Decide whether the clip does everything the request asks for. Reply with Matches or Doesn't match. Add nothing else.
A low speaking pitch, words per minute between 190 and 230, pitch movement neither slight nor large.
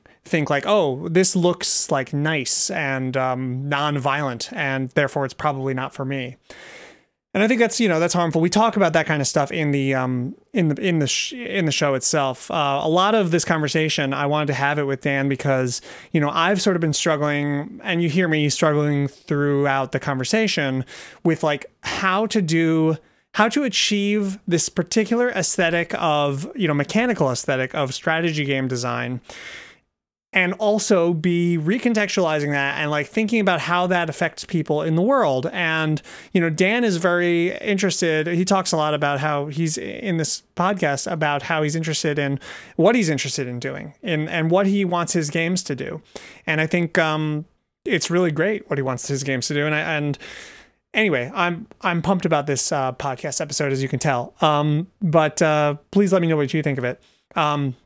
Doesn't match